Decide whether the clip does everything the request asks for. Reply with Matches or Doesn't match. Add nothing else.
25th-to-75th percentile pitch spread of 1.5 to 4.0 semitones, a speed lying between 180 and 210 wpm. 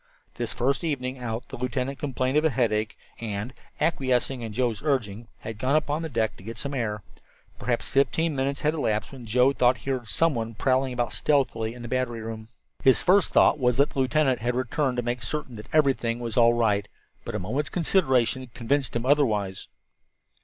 Matches